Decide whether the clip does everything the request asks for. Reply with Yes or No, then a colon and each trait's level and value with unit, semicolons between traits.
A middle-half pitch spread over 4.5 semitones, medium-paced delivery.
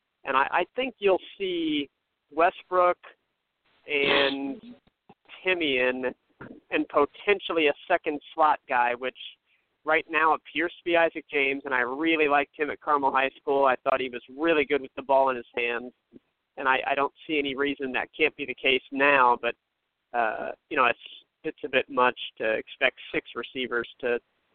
No: average, 3.7 semitones; average, 175 wpm